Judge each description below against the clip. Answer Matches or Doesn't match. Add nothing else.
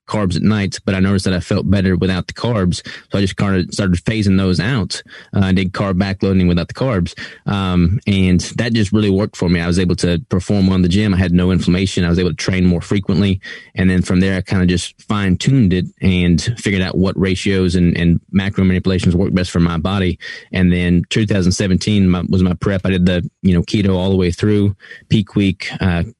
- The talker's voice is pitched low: Matches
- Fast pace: Matches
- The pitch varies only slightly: Matches